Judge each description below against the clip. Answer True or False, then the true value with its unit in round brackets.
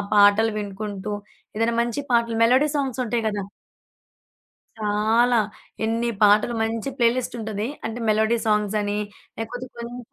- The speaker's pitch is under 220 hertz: False (225 Hz)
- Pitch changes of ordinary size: False (2.1 semitones)